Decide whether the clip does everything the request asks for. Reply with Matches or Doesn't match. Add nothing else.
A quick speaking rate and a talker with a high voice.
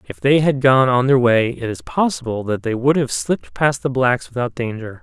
Doesn't match